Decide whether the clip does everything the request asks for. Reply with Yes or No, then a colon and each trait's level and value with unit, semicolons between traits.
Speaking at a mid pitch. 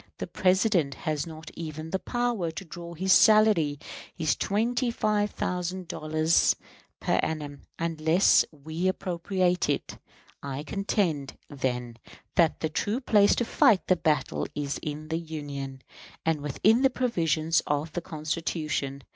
Yes: medium, 165 Hz